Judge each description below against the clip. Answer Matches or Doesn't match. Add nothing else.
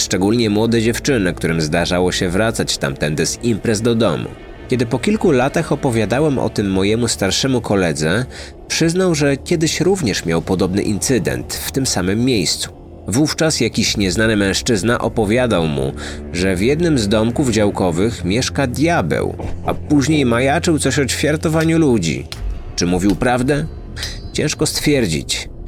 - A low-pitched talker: Matches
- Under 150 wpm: Matches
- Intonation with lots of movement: Matches